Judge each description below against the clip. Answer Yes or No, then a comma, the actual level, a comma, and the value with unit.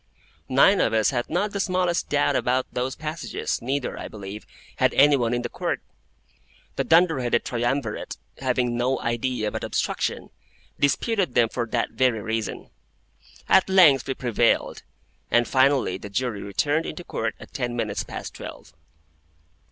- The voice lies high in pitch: No, low, 125 Hz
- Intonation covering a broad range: No, average, 3.8 semitones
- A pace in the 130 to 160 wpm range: Yes, average, 155 wpm